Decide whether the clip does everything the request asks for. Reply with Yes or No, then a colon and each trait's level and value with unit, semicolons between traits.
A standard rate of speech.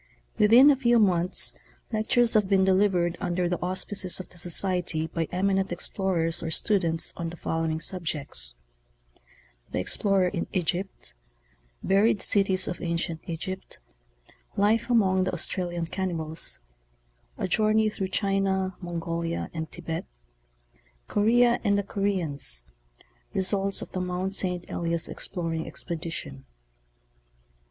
No: slow, 120 wpm